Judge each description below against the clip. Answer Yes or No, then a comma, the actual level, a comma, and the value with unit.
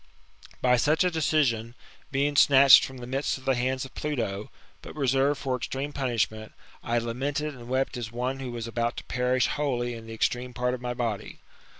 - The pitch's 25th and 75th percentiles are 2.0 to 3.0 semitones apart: Yes, narrow, 2.4 semitones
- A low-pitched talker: Yes, low, 125 Hz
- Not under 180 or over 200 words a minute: Yes, average, 190 wpm